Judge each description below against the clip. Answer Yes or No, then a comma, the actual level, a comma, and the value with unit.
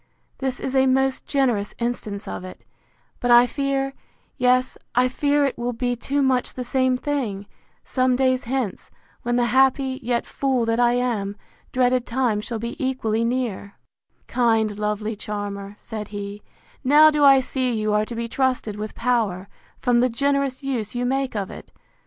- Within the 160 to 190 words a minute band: Yes, average, 170 wpm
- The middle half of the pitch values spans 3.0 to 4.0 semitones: Yes, average, 3.3 semitones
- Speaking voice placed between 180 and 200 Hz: No, high, 245 Hz